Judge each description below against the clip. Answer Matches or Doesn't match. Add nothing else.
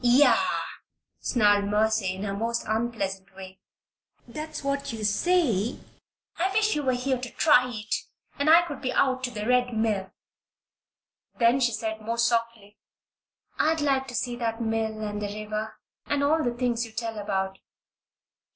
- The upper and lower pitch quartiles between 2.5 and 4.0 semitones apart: Matches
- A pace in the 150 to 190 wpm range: Matches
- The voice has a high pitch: Matches